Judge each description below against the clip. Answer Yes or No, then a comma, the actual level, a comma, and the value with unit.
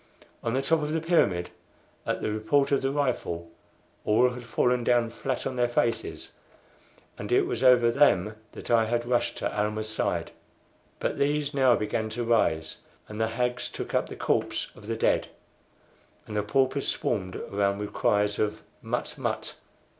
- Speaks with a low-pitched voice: Yes, low, 115 Hz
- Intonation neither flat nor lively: Yes, average, 3.7 semitones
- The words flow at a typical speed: Yes, average, 170 wpm